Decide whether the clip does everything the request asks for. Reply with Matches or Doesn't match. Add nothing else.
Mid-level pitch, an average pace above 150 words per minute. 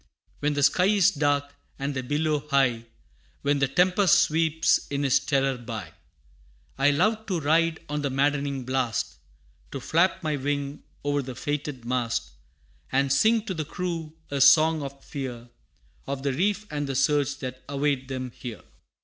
Matches